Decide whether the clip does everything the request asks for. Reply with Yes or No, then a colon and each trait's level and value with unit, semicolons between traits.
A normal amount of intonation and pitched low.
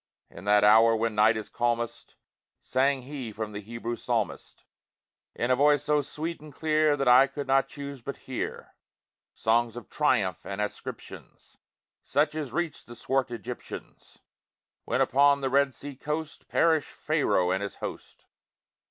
Yes: average, 4.1 semitones; low, 130 Hz